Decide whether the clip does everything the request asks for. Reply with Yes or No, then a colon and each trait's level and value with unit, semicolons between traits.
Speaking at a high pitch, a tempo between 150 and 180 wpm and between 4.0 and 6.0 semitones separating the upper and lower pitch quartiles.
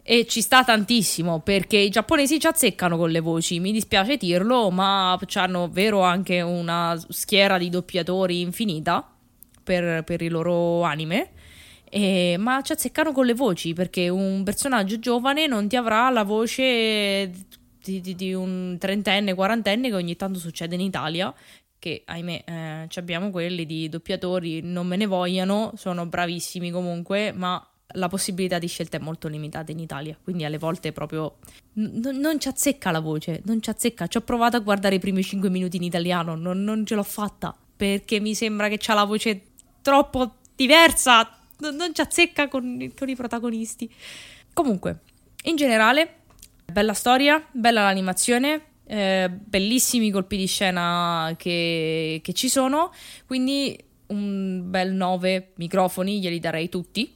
Yes: high, 195 Hz; average, 160 wpm; average, 4.6 semitones